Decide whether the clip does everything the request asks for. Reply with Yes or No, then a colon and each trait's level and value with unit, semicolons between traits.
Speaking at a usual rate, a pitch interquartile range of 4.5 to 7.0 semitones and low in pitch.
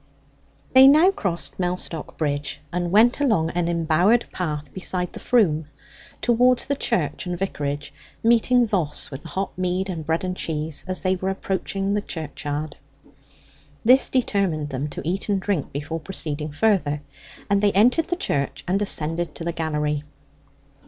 No: average, 160 wpm; average, 4.9 semitones; medium, 180 Hz